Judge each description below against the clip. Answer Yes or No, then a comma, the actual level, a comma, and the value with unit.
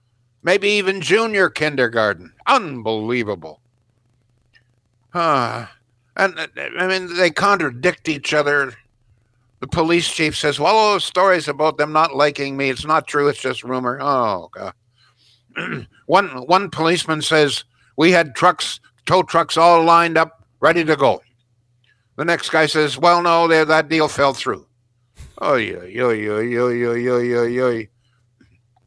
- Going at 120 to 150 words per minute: Yes, slow, 135 wpm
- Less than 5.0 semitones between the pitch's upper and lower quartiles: No, average, 5.3 semitones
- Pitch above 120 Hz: Yes, medium, 140 Hz